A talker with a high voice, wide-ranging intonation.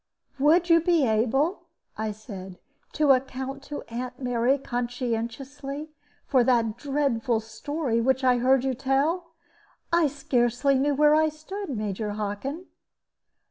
No: very high, 265 Hz; average, 3.9 semitones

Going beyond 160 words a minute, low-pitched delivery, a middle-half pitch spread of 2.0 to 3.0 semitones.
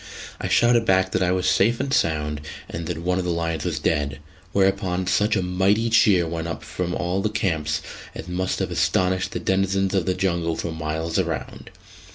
Yes: average, 200 wpm; very low, 90 Hz; narrow, 2.6 semitones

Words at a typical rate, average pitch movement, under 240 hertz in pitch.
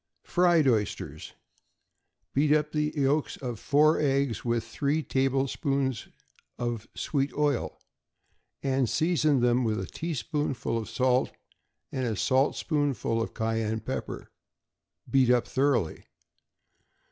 No: slow, 110 wpm; average, 3.7 semitones; low, 135 Hz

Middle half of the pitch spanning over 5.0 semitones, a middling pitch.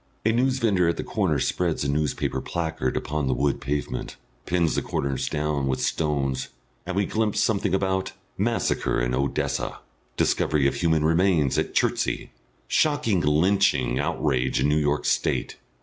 No: wide, 5.4 semitones; very low, 75 Hz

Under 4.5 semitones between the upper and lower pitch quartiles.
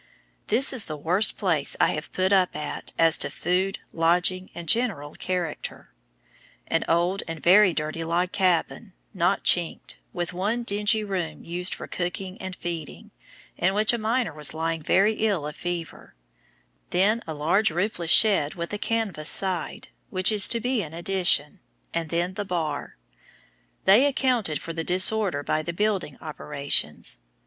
Yes: average, 3.9 semitones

